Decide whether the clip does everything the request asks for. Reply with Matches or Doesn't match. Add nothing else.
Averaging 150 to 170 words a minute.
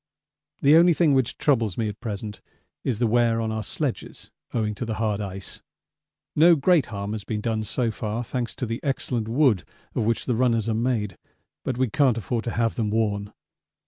Doesn't match